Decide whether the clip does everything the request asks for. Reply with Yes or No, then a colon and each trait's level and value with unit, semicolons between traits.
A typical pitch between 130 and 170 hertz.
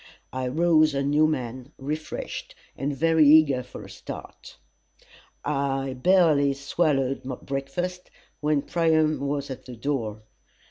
Yes: medium, 140 Hz